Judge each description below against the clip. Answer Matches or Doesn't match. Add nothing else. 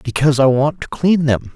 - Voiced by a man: Matches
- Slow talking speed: Doesn't match